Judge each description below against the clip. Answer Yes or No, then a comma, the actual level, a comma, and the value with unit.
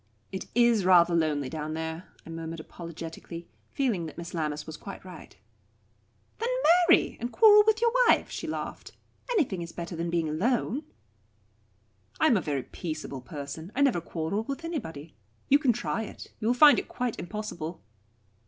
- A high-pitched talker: No, medium, 175 Hz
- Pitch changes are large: Yes, wide, 7.0 semitones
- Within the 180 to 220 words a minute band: No, average, 170 wpm